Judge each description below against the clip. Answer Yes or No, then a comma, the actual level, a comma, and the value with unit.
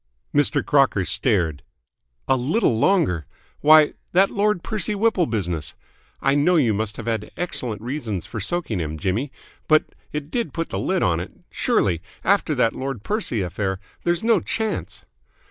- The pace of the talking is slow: No, average, 160 wpm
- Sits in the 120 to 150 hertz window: Yes, low, 135 Hz